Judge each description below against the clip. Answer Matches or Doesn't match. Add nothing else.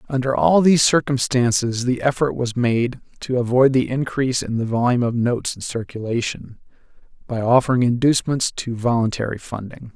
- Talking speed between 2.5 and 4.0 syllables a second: Doesn't match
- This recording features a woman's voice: Doesn't match